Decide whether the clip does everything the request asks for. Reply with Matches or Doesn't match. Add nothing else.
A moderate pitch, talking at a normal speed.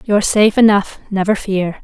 Doesn't match